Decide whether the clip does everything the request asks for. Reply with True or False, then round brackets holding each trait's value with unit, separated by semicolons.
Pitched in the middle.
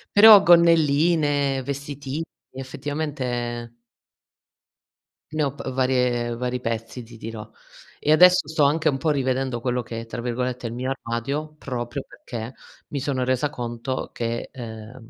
False (130 Hz)